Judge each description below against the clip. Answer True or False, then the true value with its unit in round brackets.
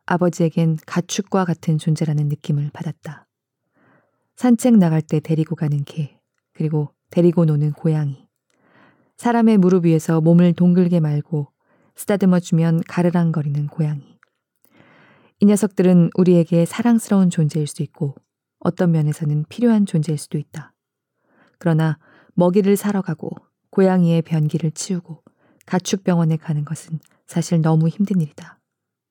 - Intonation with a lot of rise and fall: False (2.7 semitones)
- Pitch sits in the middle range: True (165 Hz)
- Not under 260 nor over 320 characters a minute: True (305 characters per minute)